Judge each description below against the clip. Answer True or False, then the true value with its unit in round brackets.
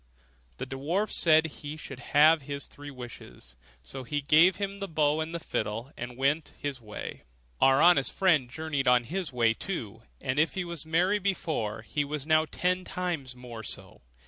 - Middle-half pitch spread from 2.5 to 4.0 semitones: False (4.5 semitones)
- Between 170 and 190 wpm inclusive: True (175 wpm)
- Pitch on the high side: False (145 Hz)